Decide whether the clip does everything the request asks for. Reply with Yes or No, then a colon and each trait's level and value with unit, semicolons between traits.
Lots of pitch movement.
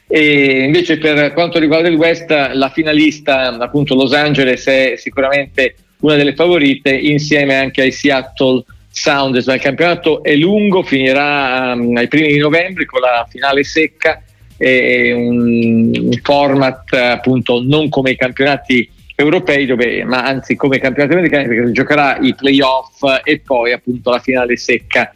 No: average, 2.7 semitones